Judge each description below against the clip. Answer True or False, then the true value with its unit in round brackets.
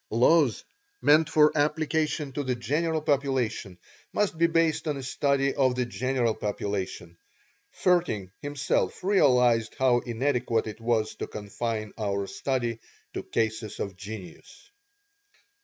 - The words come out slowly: True (125 wpm)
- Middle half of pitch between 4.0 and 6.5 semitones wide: True (5.2 semitones)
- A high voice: False (125 Hz)